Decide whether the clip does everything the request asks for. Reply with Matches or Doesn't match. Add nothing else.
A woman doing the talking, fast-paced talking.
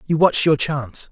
Doesn't match